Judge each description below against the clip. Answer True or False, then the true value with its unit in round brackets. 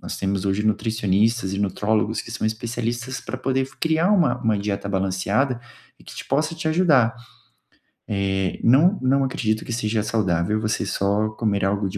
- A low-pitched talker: True (110 Hz)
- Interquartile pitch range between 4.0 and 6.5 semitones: True (4.3 semitones)